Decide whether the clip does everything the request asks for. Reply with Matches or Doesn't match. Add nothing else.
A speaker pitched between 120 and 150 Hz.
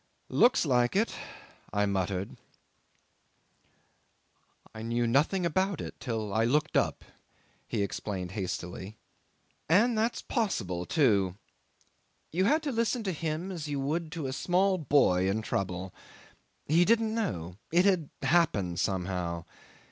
Matches